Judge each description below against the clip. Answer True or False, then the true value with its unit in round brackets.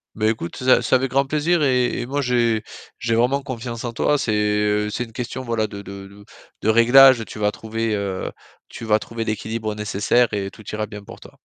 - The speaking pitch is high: False (115 Hz)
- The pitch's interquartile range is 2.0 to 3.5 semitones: True (3.0 semitones)